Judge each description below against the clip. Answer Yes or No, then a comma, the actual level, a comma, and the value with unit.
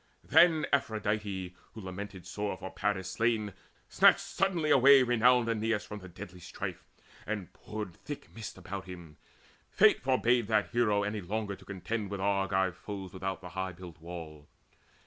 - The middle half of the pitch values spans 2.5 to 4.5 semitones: Yes, average, 3.3 semitones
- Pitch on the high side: No, low, 100 Hz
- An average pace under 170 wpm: Yes, average, 155 wpm